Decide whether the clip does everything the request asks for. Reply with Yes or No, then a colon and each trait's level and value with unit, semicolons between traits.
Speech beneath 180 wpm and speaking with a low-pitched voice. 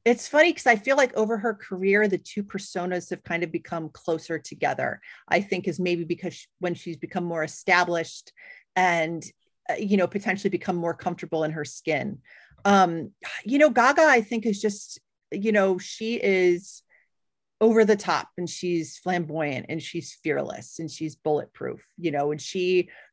No: average, 170 wpm; medium, 180 Hz